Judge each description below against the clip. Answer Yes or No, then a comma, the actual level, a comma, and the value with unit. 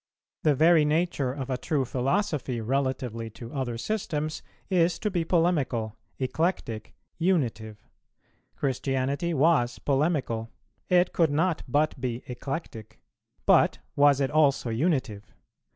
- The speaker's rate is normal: No, slow, 120 wpm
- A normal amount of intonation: Yes, average, 4.8 semitones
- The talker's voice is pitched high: No, medium, 140 Hz